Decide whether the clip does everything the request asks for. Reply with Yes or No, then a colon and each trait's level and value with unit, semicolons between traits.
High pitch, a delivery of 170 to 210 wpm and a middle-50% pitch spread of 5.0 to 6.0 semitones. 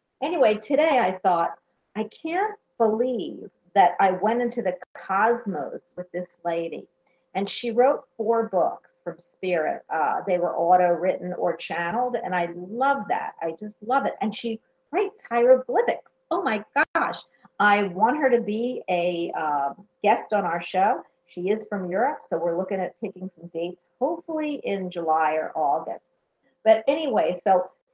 No: high, 205 Hz; average, 160 wpm; average, 5.3 semitones